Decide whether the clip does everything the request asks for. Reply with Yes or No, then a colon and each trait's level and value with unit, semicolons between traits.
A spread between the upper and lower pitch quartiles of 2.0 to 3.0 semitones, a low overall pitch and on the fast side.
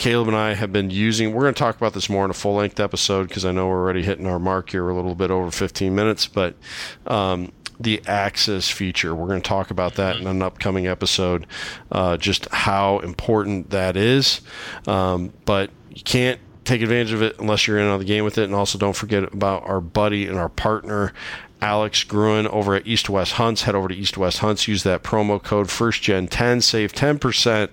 Yes: narrow, 2.4 semitones; low, 100 Hz; fast, 225 wpm